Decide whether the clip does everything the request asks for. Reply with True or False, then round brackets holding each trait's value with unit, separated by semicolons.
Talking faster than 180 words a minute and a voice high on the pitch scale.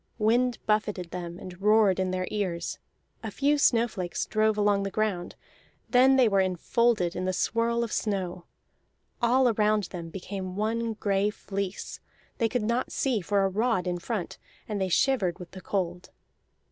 False (165 wpm; 205 Hz)